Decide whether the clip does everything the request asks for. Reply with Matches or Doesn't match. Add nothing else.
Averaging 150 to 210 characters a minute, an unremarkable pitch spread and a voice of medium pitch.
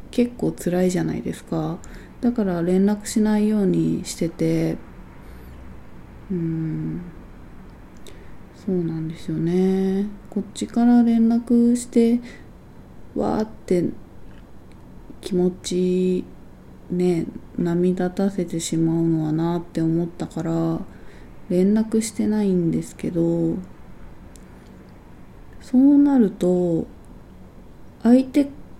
Matches